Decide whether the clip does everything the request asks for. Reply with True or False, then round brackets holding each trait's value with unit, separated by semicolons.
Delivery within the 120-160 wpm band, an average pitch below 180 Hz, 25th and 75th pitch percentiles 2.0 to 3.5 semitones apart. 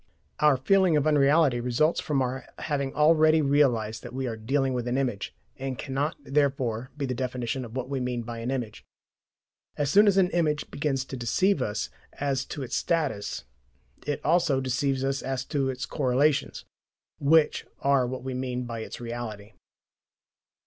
False (170 wpm; 135 Hz; 3.0 semitones)